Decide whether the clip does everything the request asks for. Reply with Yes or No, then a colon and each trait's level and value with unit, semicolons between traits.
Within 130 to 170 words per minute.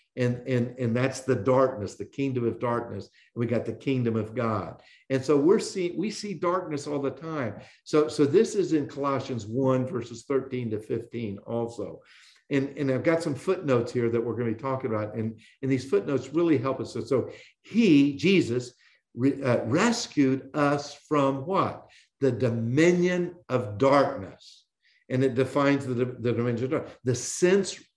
No: average, 180 wpm